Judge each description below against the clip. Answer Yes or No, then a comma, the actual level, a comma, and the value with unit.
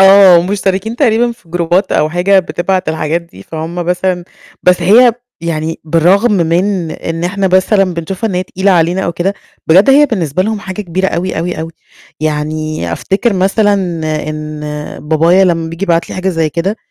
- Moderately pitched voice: Yes, medium, 180 Hz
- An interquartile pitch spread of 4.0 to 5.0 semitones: No, average, 2.9 semitones